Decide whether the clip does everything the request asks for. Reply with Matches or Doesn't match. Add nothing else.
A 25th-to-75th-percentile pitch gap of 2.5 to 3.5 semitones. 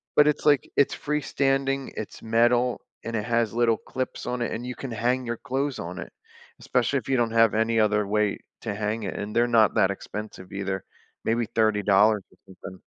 Matches